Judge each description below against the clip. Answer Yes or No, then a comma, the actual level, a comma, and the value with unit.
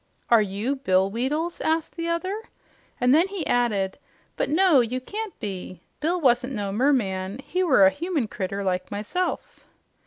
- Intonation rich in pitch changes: Yes, wide, 8.8 semitones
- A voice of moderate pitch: No, very high, 255 Hz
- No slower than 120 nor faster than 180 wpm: Yes, average, 160 wpm